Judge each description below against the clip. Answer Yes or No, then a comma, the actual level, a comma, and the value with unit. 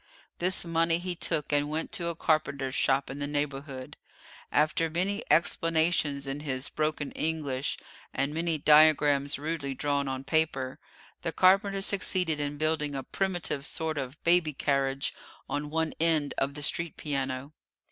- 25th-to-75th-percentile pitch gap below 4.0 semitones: Yes, average, 2.9 semitones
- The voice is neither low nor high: Yes, medium, 150 Hz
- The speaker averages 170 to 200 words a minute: No, average, 150 wpm